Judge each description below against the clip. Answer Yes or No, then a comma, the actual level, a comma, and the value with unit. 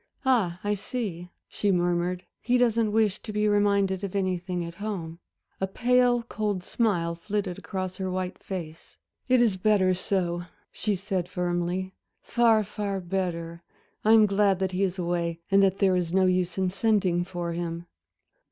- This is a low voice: No, high, 190 Hz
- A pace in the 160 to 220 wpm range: Yes, average, 165 wpm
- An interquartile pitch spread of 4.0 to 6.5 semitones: No, average, 2.9 semitones